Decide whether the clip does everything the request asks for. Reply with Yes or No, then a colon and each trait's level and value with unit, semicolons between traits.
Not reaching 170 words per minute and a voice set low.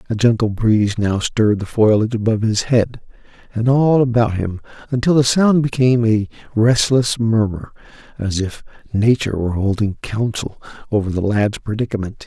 Yes: average, 150 wpm; low, 110 Hz